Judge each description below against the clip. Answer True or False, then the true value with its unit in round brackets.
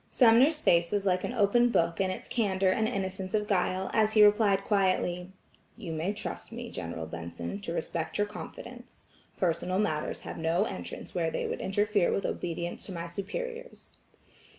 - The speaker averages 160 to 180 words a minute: True (175 wpm)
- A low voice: False (195 Hz)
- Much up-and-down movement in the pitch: False (3.8 semitones)